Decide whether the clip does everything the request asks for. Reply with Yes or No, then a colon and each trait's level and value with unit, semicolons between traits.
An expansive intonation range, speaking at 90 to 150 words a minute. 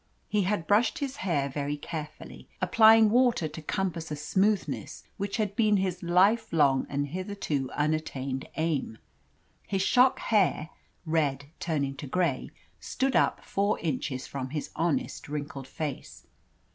Yes: wide, 5.9 semitones; average, 140 wpm